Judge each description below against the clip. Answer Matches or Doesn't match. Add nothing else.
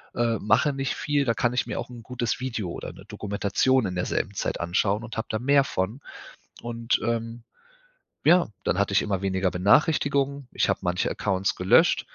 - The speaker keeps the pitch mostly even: Doesn't match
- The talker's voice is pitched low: Matches